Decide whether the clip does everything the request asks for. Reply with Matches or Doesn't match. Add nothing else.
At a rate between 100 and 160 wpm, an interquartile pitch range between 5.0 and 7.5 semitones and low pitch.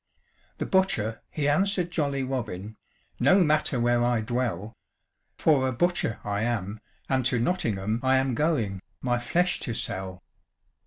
Matches